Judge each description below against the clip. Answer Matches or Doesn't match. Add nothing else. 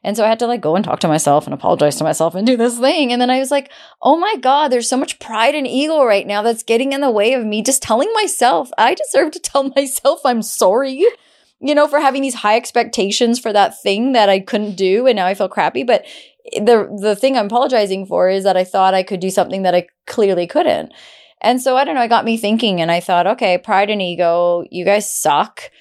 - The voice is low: Doesn't match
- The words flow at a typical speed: Doesn't match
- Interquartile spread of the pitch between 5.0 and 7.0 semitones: Matches